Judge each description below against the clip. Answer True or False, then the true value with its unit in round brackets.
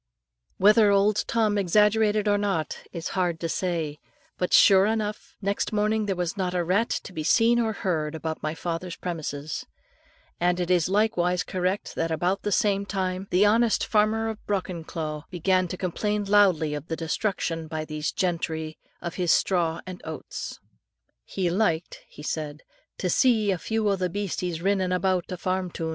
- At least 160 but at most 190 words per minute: True (175 wpm)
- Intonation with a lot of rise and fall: False (3.7 semitones)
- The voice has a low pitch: False (185 Hz)